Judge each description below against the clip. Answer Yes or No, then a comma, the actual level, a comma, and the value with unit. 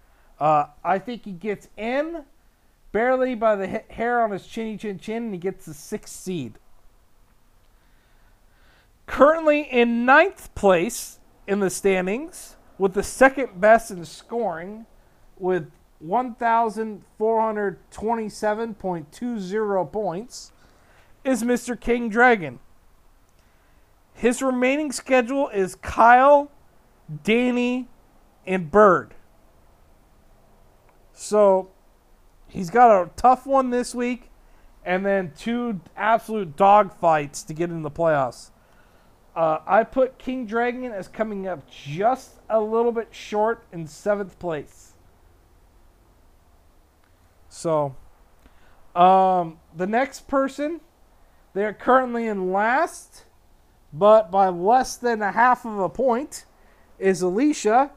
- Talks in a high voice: Yes, high, 200 Hz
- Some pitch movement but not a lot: No, wide, 7.2 semitones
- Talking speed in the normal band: No, slow, 110 wpm